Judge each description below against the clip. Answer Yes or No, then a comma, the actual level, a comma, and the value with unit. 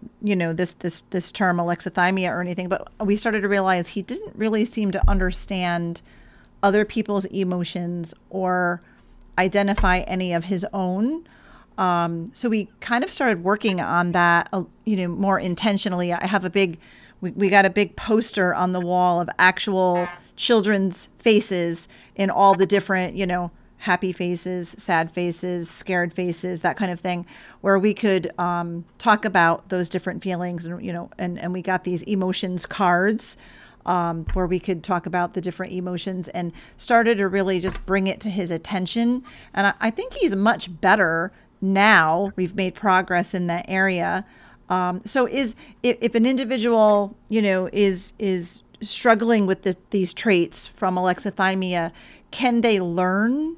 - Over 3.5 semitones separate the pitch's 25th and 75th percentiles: No, narrow, 2.5 semitones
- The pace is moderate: Yes, average, 165 wpm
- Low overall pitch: No, medium, 185 Hz